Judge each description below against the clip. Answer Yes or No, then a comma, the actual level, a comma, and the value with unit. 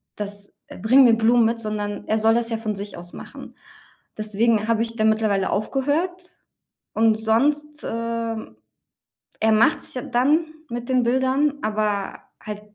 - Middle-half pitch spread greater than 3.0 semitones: No, narrow, 2.4 semitones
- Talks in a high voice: Yes, high, 225 Hz